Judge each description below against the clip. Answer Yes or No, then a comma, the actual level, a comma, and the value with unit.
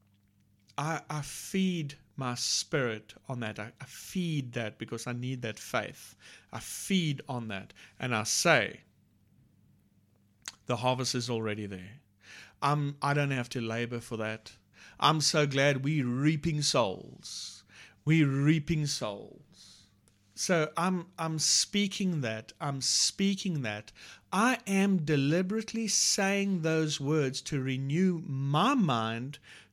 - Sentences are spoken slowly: Yes, slow, 125 wpm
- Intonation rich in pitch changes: Yes, wide, 6.1 semitones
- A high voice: No, low, 135 Hz